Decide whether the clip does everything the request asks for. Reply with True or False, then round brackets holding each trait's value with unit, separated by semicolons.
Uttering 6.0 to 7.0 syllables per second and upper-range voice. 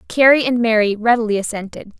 True (6.2 syllables/s; 225 Hz)